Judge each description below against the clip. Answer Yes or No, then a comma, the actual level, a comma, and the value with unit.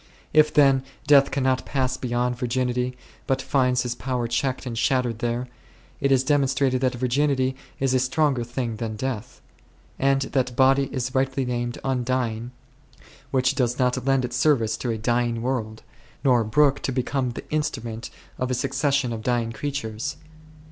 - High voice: No, low, 130 Hz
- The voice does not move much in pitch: Yes, narrow, 1.9 semitones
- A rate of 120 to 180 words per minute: Yes, average, 165 wpm